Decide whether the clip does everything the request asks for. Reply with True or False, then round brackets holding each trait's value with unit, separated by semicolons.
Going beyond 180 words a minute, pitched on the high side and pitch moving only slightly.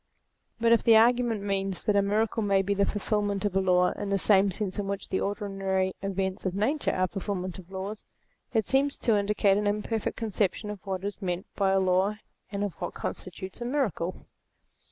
True (200 wpm; 200 Hz; 1.8 semitones)